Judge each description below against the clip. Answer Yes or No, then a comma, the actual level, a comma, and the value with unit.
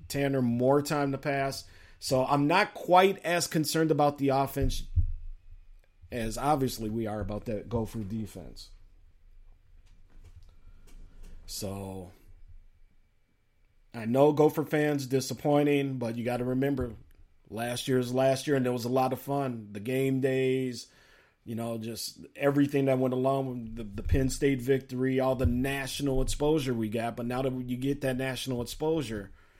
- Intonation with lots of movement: Yes, wide, 5.8 semitones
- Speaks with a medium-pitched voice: No, low, 125 Hz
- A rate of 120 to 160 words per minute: Yes, average, 150 wpm